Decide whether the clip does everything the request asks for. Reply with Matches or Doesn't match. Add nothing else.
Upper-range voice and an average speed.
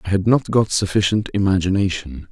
Doesn't match